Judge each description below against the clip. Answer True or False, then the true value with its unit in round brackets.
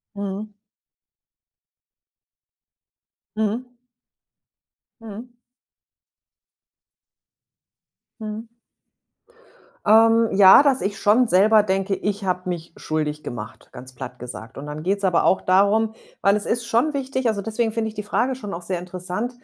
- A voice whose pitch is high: True (205 Hz)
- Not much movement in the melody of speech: False (3.7 semitones)